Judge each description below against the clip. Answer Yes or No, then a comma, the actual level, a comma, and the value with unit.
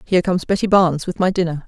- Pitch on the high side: No, medium, 180 Hz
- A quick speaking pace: Yes, fast, 250 wpm